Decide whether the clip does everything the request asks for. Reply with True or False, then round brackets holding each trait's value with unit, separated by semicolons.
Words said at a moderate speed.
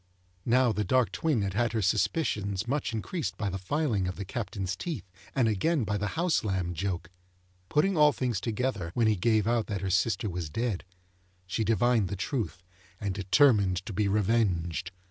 True (185 wpm)